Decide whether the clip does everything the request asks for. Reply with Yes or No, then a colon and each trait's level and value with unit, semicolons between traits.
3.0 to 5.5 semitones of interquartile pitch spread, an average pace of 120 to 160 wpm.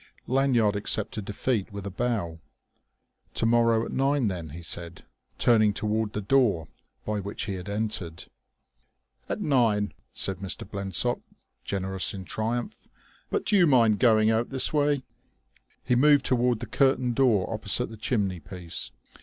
Yes: average, 3.9 semitones; average, 150 wpm